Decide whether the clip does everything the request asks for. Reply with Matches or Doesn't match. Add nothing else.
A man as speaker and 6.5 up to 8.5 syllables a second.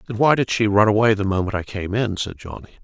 Matches